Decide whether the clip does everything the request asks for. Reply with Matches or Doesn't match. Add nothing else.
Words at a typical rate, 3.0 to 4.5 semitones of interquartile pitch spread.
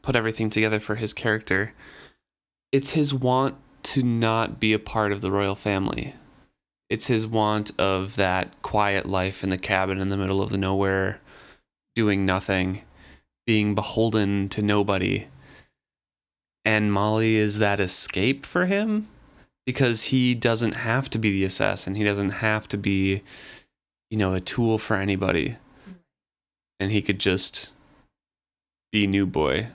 Doesn't match